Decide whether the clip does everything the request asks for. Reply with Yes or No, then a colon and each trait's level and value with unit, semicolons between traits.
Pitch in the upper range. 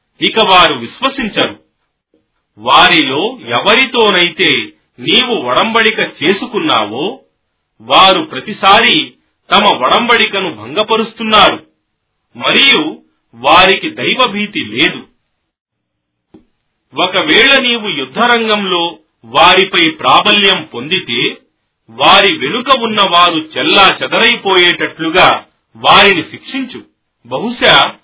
Yes: high, 215 Hz